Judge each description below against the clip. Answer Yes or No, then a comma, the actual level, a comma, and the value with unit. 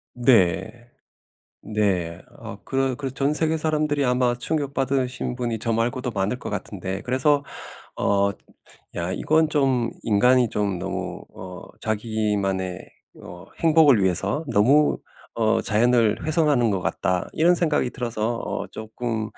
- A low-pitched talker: Yes, low, 120 Hz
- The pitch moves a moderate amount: Yes, average, 4.9 semitones